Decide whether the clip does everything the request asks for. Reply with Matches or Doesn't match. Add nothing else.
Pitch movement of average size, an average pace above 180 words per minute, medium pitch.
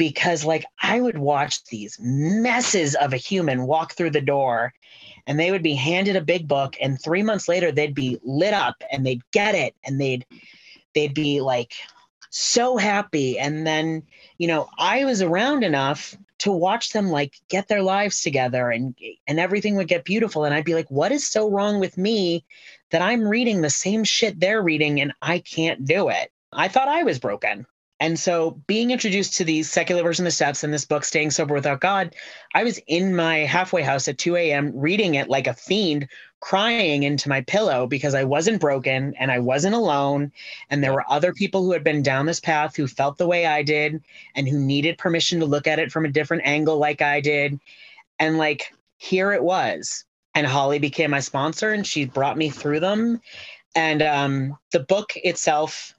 Matches